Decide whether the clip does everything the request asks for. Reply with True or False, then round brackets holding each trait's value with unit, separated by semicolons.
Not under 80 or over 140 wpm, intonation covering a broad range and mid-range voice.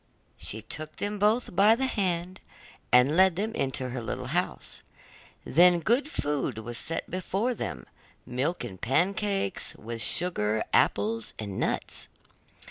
True (135 wpm; 8.6 semitones; 165 Hz)